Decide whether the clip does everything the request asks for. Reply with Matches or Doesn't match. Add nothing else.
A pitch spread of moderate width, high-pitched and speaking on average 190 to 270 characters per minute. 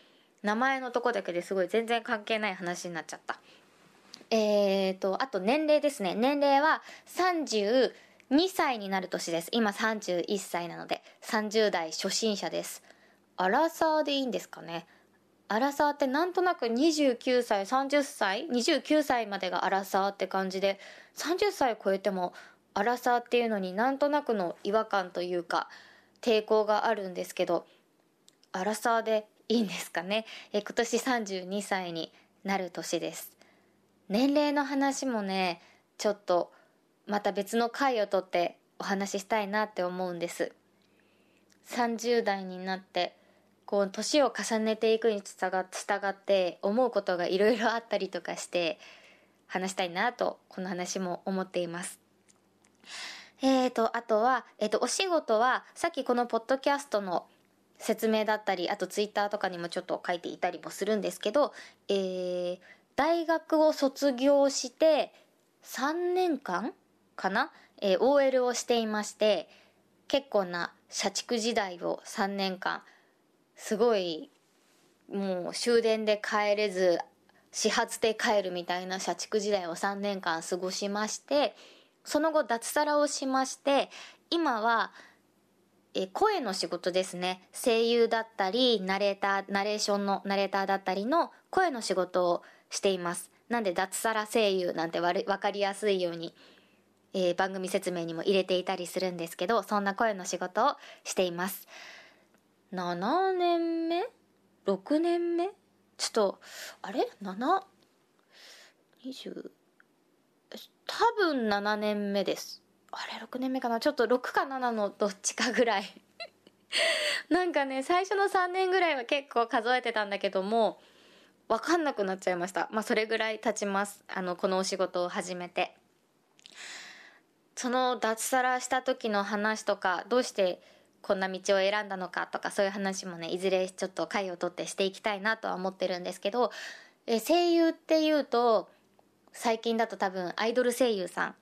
Doesn't match